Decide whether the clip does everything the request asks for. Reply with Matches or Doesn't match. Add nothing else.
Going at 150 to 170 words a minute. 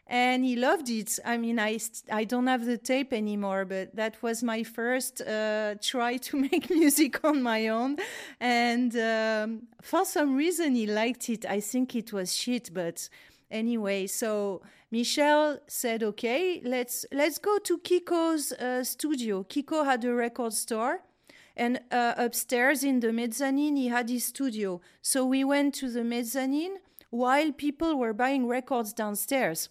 Matches